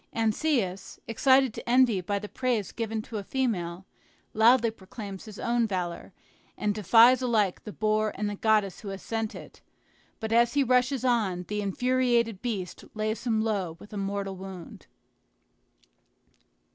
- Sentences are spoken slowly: No, average, 155 wpm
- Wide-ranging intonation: No, average, 3.3 semitones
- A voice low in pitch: No, high, 215 Hz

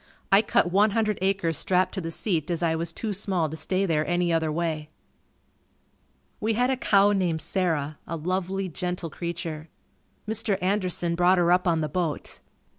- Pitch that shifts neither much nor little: Yes, average, 3.0 semitones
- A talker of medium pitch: Yes, medium, 180 Hz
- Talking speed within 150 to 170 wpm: No, average, 180 wpm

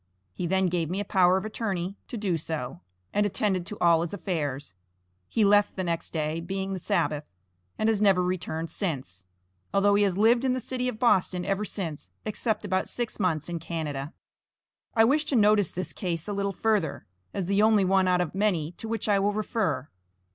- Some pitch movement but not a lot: Yes, average, 3.8 semitones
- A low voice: No, high, 190 Hz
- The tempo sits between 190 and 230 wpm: Yes, average, 200 wpm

